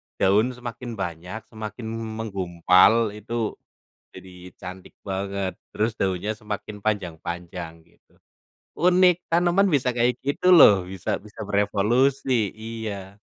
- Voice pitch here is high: No, low, 105 Hz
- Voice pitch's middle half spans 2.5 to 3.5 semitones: No, average, 4.1 semitones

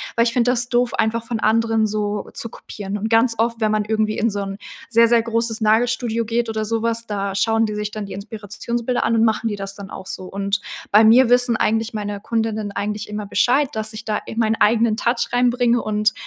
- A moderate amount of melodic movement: No, narrow, 1.7 semitones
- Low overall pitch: No, high, 220 Hz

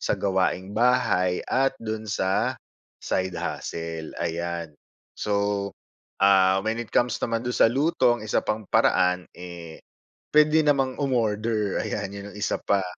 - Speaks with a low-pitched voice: Yes, low, 105 Hz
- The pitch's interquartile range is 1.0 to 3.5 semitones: No, average, 4.2 semitones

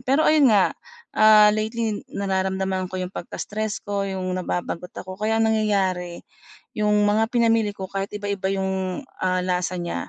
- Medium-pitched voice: No, high, 200 Hz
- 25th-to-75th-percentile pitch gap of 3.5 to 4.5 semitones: No, narrow, 2.5 semitones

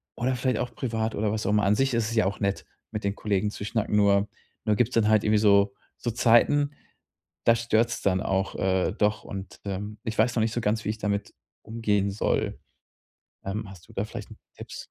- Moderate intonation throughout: No, narrow, 2.3 semitones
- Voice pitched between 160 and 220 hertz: No, low, 105 Hz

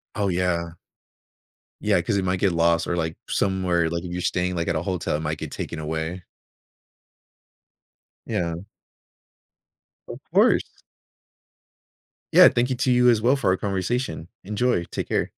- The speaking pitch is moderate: No, very low, 90 Hz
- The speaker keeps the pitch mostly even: No, average, 3.2 semitones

